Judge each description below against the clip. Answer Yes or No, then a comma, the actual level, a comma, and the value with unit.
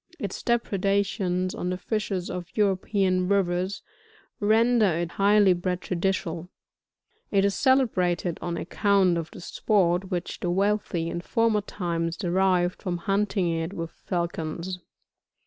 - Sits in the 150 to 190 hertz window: Yes, medium, 185 Hz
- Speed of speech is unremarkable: No, slow, 125 wpm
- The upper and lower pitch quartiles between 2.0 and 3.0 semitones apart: Yes, narrow, 2.4 semitones